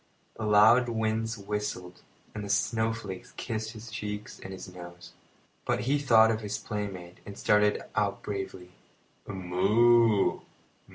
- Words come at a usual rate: No, slow, 130 wpm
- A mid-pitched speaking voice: No, low, 105 Hz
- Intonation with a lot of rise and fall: No, narrow, 2.5 semitones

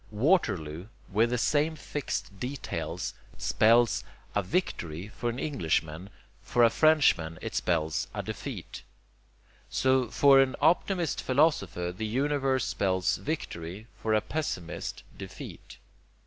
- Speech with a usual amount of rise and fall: No, wide, 7.8 semitones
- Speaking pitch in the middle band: No, low, 115 Hz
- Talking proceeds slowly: Yes, slow, 120 wpm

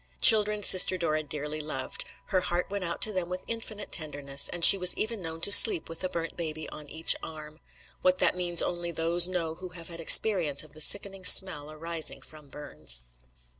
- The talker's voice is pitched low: No, medium, 170 Hz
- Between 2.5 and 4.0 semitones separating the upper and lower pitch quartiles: Yes, average, 3.2 semitones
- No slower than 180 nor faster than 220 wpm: Yes, average, 200 wpm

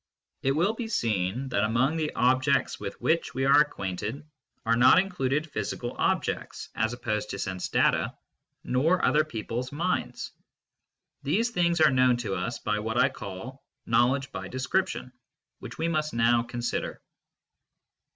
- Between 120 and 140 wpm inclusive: No, average, 150 wpm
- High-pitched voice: No, low, 130 Hz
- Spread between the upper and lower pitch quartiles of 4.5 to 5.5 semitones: Yes, average, 4.9 semitones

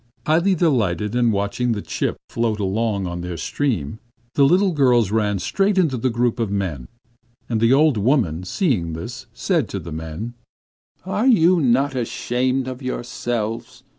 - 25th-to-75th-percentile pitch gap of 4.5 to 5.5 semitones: Yes, average, 5.2 semitones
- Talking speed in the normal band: Yes, average, 160 wpm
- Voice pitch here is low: Yes, low, 120 Hz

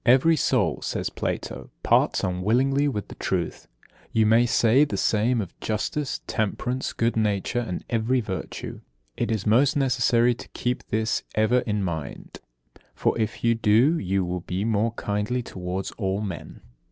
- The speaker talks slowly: No, average, 155 wpm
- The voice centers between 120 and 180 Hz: No, low, 110 Hz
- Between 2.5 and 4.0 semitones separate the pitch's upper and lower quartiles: Yes, average, 3.3 semitones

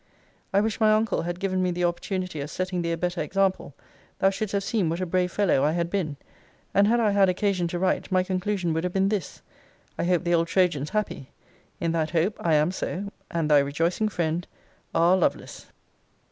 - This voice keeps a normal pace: No, fast, 210 wpm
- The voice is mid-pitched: Yes, medium, 180 Hz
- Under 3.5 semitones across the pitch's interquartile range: Yes, average, 2.7 semitones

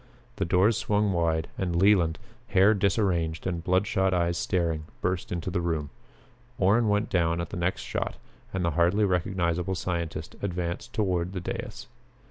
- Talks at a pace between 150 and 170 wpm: Yes, average, 155 wpm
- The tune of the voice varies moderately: No, narrow, 2.3 semitones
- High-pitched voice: No, very low, 90 Hz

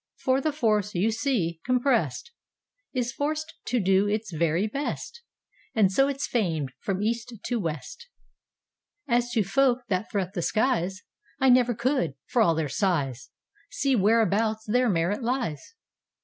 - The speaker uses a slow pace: Yes, slow, 130 wpm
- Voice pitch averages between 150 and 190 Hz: No, high, 220 Hz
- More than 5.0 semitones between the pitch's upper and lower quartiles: Yes, wide, 5.4 semitones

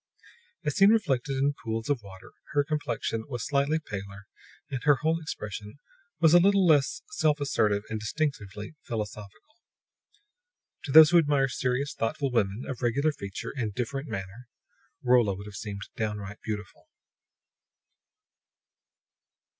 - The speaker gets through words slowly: Yes, slow, 130 wpm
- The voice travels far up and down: Yes, wide, 5.8 semitones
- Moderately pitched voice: No, low, 125 Hz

